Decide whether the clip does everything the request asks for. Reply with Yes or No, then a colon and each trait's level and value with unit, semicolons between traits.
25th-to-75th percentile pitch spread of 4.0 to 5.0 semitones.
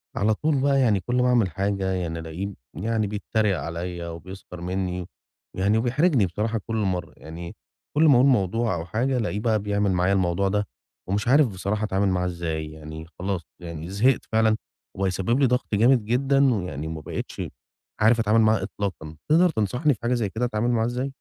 Yes: average, 4.7 semitones